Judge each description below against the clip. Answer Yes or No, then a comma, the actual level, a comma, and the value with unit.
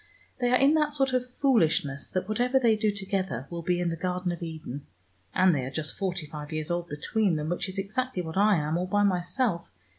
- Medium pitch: Yes, medium, 180 Hz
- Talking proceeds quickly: Yes, fast, 230 wpm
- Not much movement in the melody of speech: No, average, 5.1 semitones